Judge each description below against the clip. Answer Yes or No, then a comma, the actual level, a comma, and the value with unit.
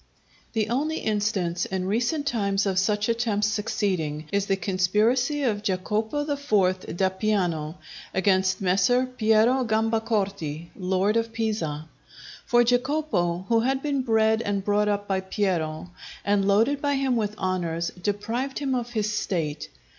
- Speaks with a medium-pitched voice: No, high, 210 Hz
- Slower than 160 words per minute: Yes, average, 140 wpm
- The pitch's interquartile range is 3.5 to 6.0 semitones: Yes, average, 3.8 semitones